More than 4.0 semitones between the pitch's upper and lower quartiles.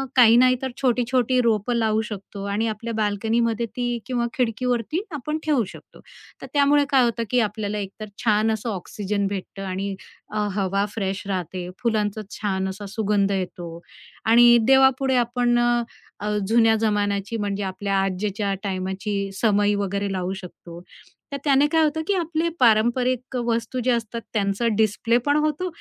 No: average, 3.6 semitones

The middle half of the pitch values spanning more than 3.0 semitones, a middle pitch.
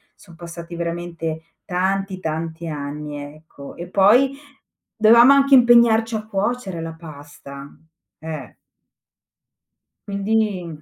Yes: average, 5.1 semitones; medium, 175 Hz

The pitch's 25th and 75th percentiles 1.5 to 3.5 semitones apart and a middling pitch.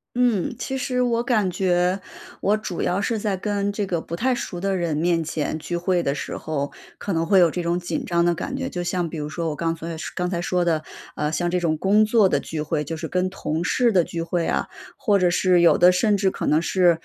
Yes: average, 3.1 semitones; medium, 180 Hz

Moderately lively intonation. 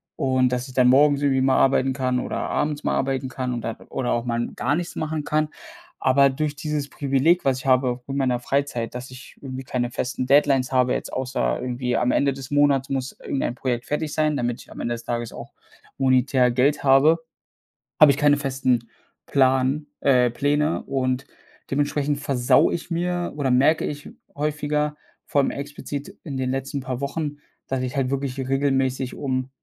No: narrow, 2.2 semitones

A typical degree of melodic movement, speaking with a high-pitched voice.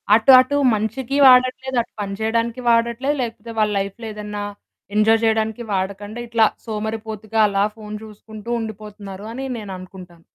No: narrow, 2.0 semitones; high, 220 Hz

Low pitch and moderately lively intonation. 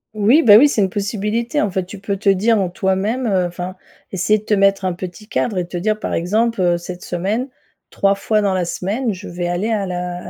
No: high, 195 Hz; average, 3.0 semitones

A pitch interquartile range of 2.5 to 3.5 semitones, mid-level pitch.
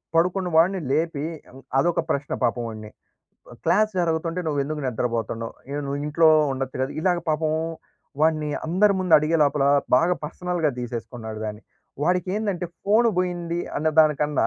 No: average, 4.4 semitones; medium, 155 Hz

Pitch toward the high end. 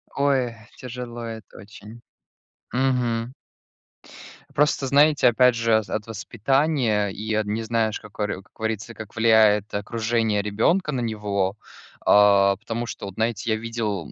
No: low, 115 Hz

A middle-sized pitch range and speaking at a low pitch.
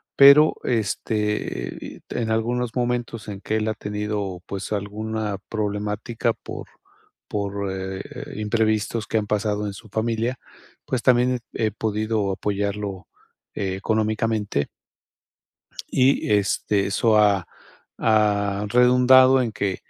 No: narrow, 2.1 semitones; low, 105 Hz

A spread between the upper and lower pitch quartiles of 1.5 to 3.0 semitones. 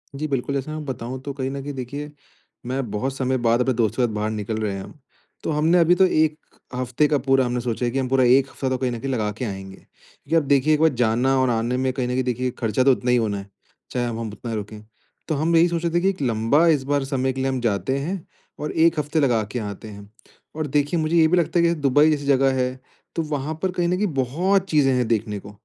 No: average, 4.0 semitones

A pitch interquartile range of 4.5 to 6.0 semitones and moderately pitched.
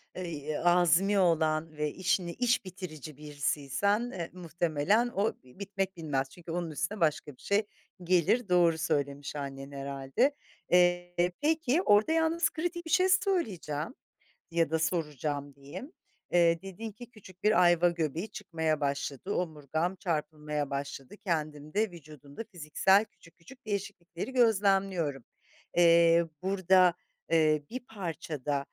Yes: average, 4.8 semitones; medium, 170 Hz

